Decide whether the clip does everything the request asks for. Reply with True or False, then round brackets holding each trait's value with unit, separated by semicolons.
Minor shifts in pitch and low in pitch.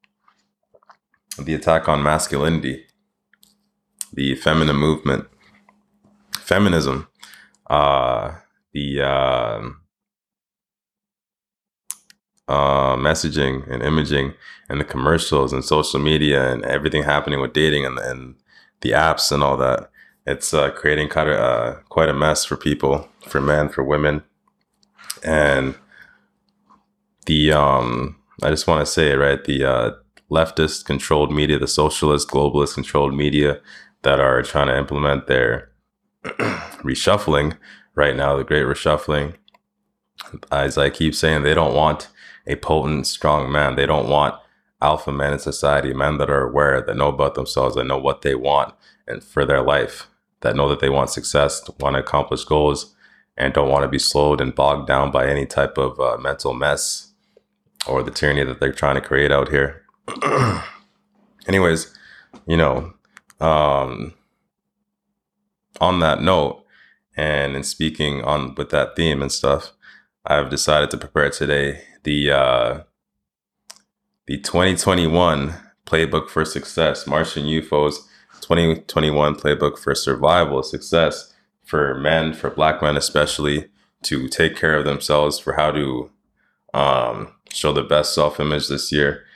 True (1.9 semitones; 75 Hz)